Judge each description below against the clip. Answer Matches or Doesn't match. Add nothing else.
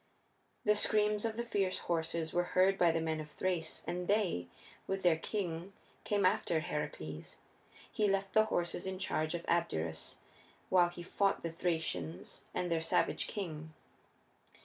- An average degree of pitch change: Matches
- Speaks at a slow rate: Doesn't match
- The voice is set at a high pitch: Doesn't match